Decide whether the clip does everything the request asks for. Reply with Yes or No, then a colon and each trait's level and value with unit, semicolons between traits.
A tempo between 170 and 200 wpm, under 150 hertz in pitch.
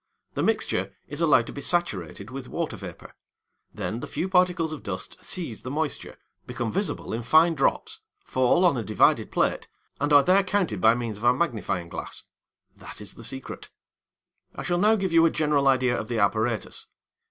Yes: average, 185 wpm; low, 135 Hz